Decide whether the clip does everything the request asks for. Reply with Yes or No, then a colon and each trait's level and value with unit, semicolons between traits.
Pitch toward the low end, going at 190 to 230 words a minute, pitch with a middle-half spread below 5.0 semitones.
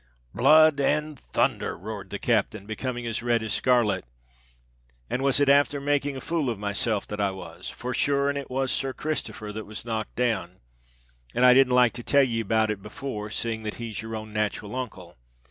Yes: low, 115 Hz; average, 195 wpm; average, 4.2 semitones